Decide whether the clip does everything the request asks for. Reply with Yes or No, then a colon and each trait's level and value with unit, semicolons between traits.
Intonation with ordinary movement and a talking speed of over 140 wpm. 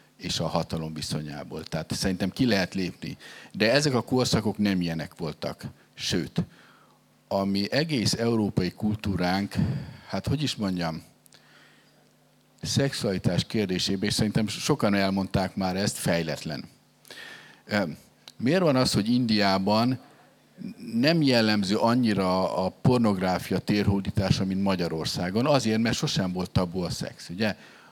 No: average, 3.9 semitones; average, 120 wpm